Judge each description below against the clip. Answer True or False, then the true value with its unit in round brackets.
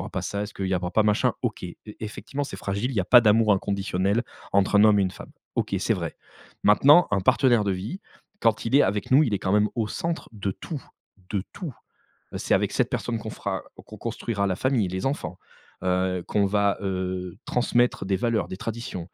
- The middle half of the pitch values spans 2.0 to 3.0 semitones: False (3.6 semitones)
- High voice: False (105 Hz)